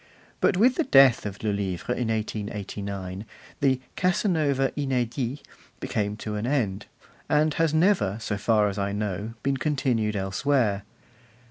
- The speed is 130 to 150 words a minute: Yes, average, 140 wpm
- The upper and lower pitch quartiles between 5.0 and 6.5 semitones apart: Yes, wide, 5.6 semitones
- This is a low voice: Yes, low, 115 Hz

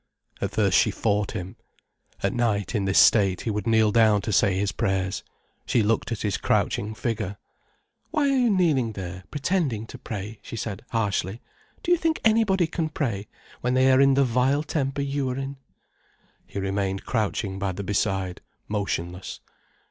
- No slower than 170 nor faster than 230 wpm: Yes, average, 175 wpm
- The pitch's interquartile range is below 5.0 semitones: No, wide, 5.5 semitones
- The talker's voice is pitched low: Yes, low, 110 Hz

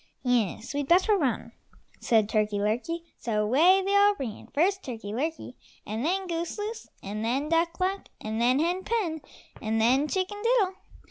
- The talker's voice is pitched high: Yes, very high, 305 Hz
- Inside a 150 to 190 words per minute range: Yes, average, 165 wpm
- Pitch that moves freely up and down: Yes, wide, 8.7 semitones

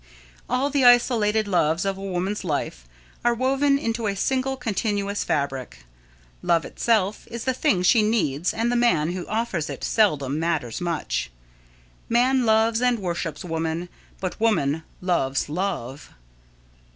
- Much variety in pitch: Yes, wide, 6.3 semitones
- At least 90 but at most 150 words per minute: Yes, average, 140 wpm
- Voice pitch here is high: Yes, high, 195 Hz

